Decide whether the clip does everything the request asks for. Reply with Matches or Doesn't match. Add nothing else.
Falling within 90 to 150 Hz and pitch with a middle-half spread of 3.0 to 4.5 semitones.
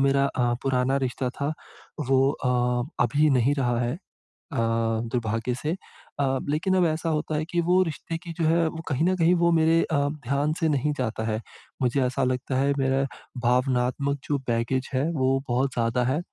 Matches